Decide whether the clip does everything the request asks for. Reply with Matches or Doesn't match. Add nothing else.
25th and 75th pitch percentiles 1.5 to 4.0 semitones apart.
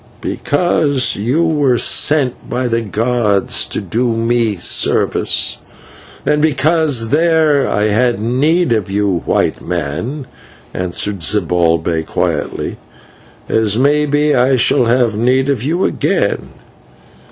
Doesn't match